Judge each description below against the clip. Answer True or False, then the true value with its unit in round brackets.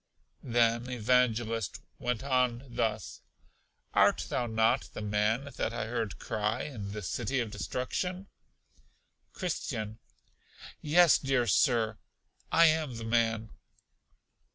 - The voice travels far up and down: False (2.6 semitones)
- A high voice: False (120 Hz)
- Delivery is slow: True (110 wpm)